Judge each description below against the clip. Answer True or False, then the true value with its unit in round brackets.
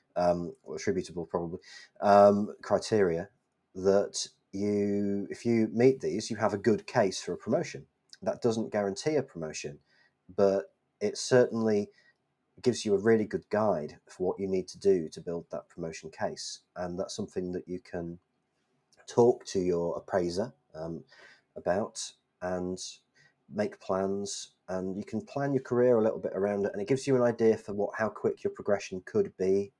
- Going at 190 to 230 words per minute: False (170 wpm)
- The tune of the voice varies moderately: True (4.5 semitones)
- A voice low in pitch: True (100 Hz)